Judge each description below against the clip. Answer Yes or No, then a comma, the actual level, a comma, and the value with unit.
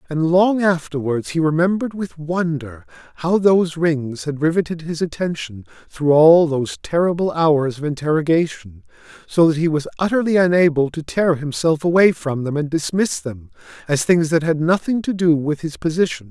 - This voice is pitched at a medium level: Yes, medium, 160 Hz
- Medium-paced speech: Yes, average, 170 wpm